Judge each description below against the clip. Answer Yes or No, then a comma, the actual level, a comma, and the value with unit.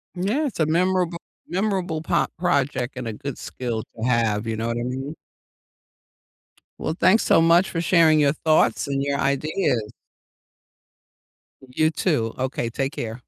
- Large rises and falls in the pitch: Yes, wide, 5.7 semitones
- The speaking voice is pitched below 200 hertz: Yes, medium, 140 Hz